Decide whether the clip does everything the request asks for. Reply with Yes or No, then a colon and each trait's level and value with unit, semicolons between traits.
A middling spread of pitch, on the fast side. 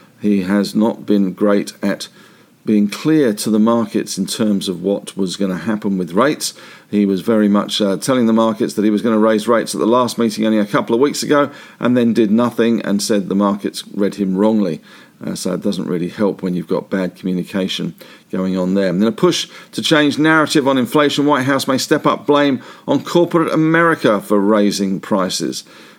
Yes: average, 4.1 semitones; fast, 210 wpm